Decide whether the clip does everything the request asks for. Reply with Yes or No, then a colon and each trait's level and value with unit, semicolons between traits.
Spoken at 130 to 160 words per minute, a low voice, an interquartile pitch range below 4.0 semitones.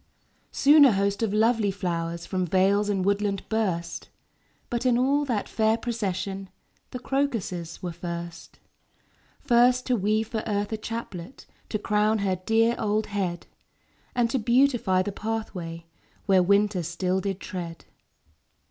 No: average, 140 wpm; high, 205 Hz; average, 3.6 semitones